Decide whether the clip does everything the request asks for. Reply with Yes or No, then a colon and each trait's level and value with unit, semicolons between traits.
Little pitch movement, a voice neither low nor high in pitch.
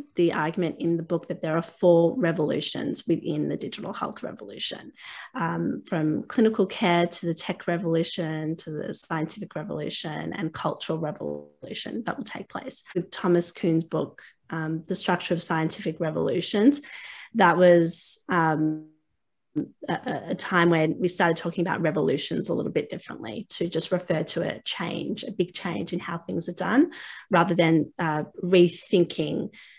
Yes: narrow, 2.0 semitones; medium, 175 Hz